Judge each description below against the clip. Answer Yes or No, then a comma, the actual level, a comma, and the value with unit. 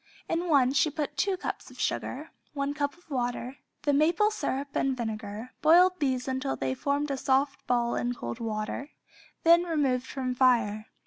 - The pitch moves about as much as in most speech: Yes, average, 3.4 semitones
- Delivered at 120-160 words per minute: No, average, 175 wpm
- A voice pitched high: Yes, very high, 275 Hz